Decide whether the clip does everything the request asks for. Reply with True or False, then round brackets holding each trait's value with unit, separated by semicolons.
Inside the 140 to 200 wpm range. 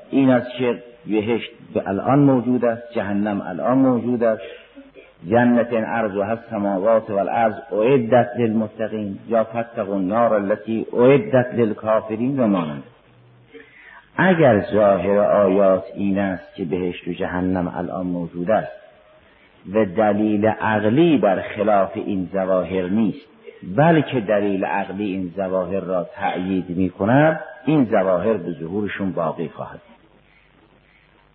False (125 wpm)